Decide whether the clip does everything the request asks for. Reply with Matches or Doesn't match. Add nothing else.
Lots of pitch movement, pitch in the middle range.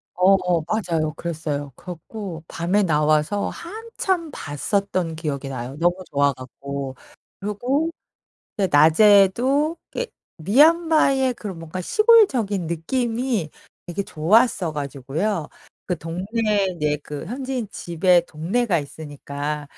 Matches